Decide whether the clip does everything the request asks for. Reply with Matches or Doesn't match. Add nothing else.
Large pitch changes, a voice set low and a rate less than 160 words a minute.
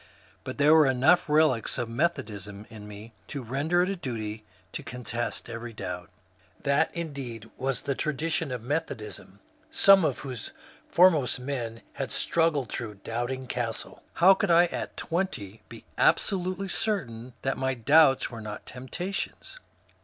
Matches